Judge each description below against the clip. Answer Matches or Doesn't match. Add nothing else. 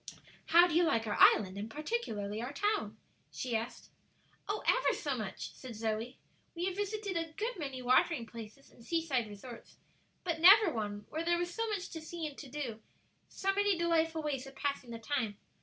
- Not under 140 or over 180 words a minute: Doesn't match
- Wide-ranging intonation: Matches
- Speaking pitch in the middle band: Doesn't match